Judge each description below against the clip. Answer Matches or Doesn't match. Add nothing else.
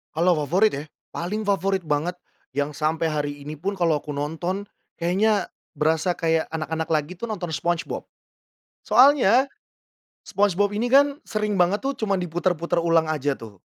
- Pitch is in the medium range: Matches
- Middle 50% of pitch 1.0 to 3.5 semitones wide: Doesn't match